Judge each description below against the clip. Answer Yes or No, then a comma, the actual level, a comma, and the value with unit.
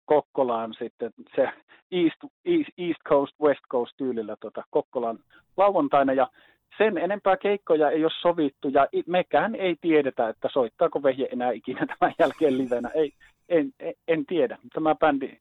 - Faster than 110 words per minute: Yes, average, 150 wpm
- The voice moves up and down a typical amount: No, wide, 6.0 semitones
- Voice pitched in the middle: Yes, medium, 150 Hz